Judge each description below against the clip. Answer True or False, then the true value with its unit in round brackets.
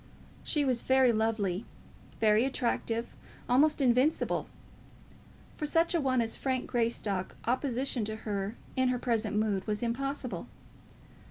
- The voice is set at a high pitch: True (240 Hz)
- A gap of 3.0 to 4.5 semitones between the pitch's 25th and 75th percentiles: True (3.3 semitones)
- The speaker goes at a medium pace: False (125 wpm)